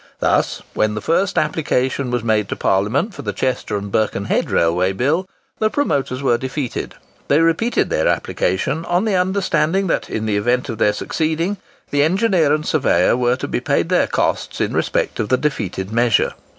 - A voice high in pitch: No, low, 130 Hz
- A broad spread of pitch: Yes, wide, 7.3 semitones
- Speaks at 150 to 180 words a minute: Yes, average, 175 wpm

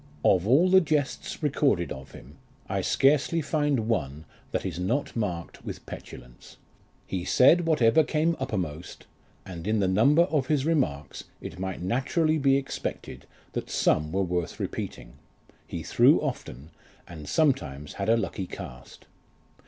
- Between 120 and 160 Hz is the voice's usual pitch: No, low, 110 Hz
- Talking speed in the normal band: Yes, average, 145 wpm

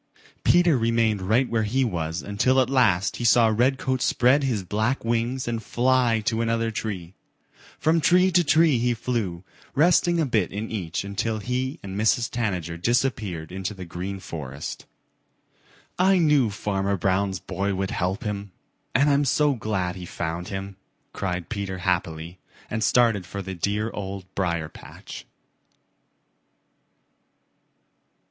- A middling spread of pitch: Yes, average, 4.8 semitones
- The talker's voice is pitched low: Yes, low, 110 Hz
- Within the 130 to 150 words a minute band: Yes, average, 145 wpm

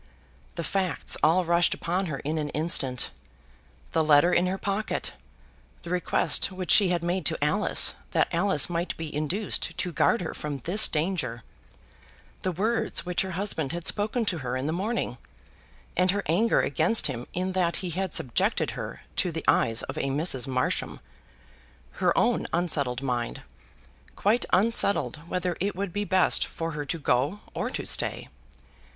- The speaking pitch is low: No, medium, 175 Hz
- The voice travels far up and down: No, average, 4.1 semitones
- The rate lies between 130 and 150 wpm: No, average, 170 wpm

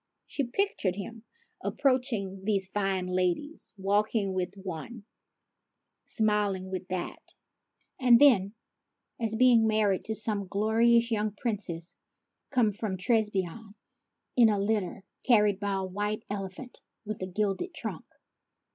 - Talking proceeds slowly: Yes, slow, 125 wpm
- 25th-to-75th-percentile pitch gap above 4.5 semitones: No, average, 2.9 semitones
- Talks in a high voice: Yes, high, 210 Hz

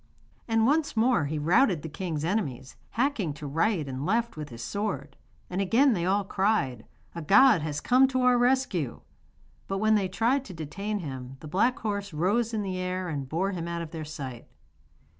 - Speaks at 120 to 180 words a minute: No, average, 195 wpm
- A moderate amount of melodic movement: No, wide, 6.6 semitones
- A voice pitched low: No, medium, 185 Hz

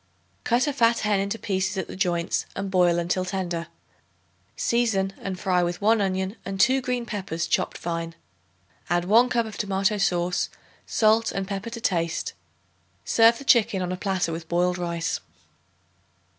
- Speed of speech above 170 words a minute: No, average, 165 wpm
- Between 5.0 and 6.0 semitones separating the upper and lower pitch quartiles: No, average, 3.8 semitones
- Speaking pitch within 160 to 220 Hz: Yes, high, 190 Hz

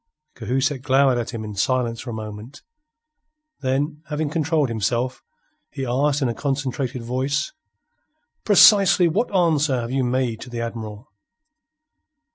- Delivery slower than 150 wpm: Yes, slow, 135 wpm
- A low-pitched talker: Yes, low, 130 Hz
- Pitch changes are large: No, average, 3.7 semitones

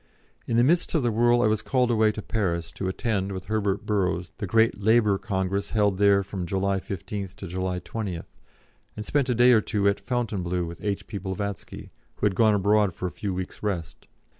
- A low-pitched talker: Yes, low, 100 Hz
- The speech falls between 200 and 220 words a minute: Yes, fast, 205 wpm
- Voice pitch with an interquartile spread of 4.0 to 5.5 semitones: No, average, 2.8 semitones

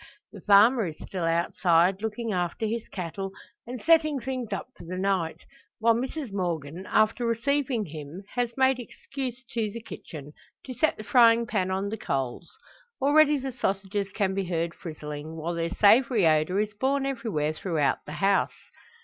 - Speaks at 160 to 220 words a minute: Yes, average, 165 wpm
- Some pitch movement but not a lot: No, wide, 6.0 semitones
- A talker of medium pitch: No, high, 200 Hz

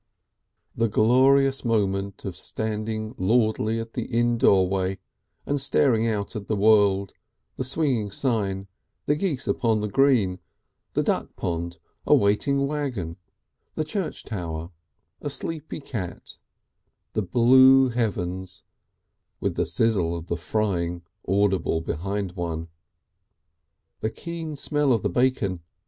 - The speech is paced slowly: Yes, slow, 125 wpm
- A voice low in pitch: Yes, low, 110 Hz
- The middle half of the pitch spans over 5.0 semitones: Yes, wide, 5.5 semitones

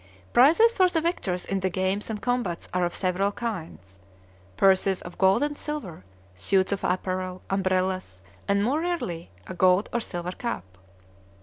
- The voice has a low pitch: No, high, 190 Hz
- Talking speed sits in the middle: Yes, average, 160 wpm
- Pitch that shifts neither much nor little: Yes, average, 4.6 semitones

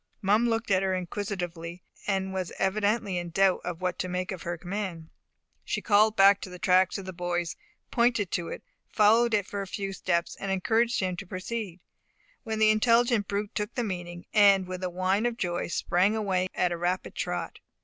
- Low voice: No, high, 190 Hz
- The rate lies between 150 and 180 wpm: No, average, 195 wpm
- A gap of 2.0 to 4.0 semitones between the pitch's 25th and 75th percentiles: Yes, average, 2.8 semitones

